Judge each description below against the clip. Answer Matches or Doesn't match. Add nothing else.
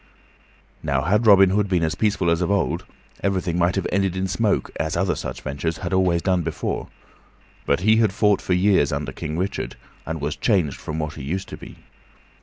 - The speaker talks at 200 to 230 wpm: Matches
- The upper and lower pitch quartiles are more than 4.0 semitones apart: Doesn't match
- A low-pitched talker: Matches